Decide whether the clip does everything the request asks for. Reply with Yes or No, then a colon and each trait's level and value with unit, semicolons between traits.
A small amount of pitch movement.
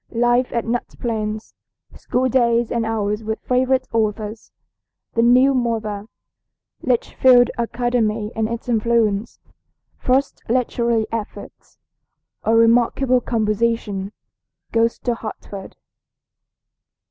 Yes: narrow, 2.0 semitones